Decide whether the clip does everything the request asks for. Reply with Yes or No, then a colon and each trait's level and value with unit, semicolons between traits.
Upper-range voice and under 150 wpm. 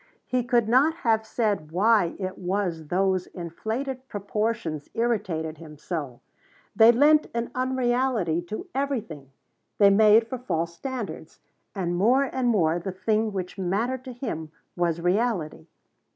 Yes: high, 210 Hz; slow, 135 wpm